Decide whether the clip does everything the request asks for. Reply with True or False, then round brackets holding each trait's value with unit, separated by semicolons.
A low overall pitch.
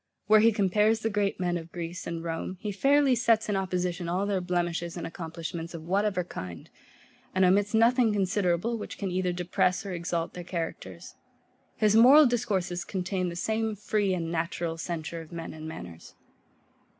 False (180 Hz)